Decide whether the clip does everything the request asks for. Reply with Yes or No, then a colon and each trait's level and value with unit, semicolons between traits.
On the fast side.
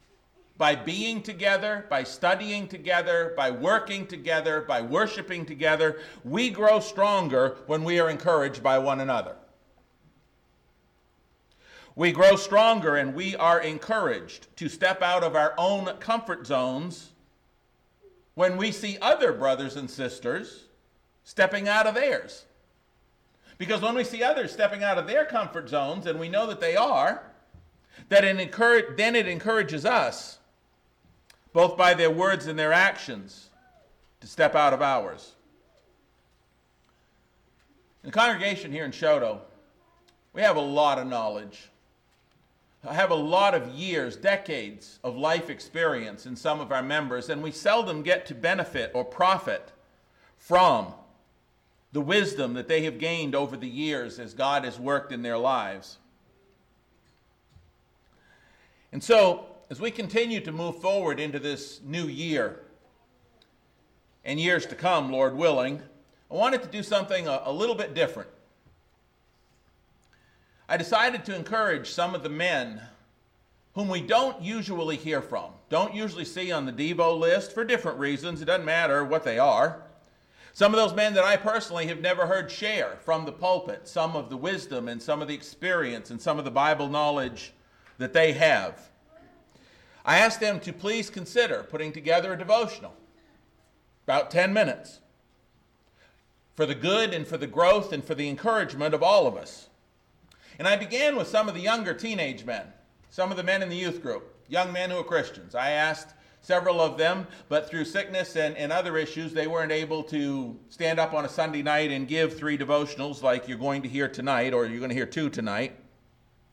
No: average, 165 wpm